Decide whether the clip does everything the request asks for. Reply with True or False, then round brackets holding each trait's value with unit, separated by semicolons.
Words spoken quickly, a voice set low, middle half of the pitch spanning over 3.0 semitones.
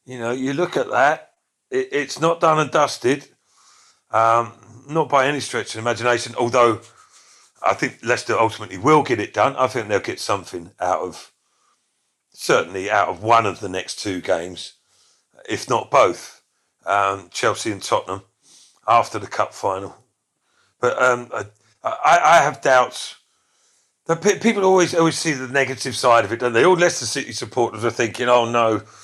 False (170 wpm; 125 Hz; 5.2 semitones)